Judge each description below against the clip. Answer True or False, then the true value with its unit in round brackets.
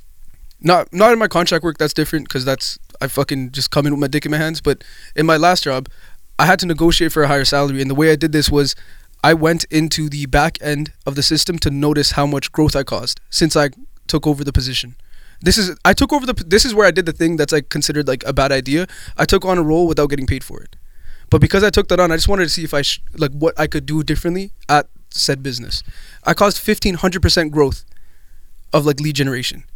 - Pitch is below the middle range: False (150 Hz)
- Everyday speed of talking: False (250 wpm)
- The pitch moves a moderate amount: True (3.3 semitones)